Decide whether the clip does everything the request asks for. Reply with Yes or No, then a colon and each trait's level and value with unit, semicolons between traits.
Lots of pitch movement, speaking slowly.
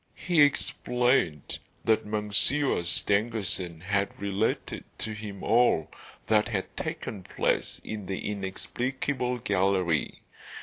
No: average, 3.8 semitones; slow, 100 wpm